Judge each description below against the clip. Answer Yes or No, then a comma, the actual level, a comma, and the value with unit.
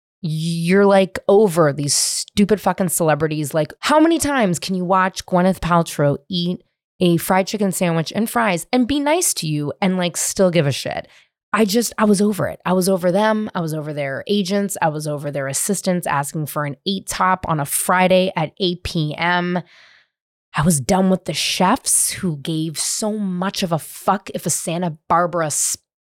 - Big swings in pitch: No, average, 3.7 semitones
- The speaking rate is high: No, average, 190 wpm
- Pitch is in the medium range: Yes, medium, 180 Hz